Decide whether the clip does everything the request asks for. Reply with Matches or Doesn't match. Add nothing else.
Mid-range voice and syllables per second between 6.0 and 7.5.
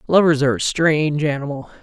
Matches